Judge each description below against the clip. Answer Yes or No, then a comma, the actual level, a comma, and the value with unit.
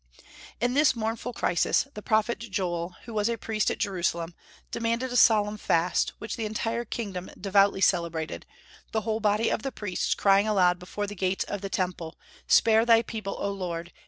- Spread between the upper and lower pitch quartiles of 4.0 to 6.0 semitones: No, average, 3.6 semitones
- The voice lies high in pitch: Yes, high, 205 Hz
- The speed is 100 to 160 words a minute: No, average, 180 wpm